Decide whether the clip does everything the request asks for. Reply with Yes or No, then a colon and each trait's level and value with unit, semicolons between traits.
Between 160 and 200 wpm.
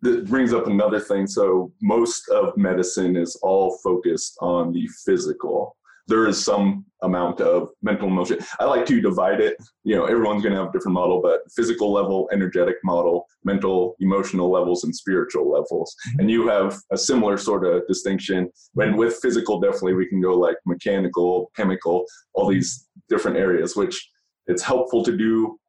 Yes: average, 175 wpm